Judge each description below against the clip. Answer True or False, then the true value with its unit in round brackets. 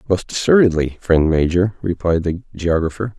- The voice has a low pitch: True (90 Hz)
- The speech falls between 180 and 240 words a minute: False (130 wpm)